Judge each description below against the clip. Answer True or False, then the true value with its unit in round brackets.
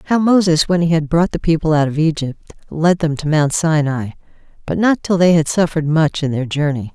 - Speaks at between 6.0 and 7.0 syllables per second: False (5.4 syllables/s)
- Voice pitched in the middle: True (160 Hz)